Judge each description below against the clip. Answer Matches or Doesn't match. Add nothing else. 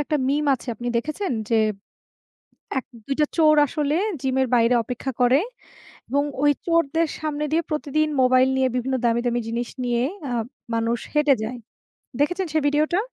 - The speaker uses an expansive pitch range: Doesn't match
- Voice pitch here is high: Matches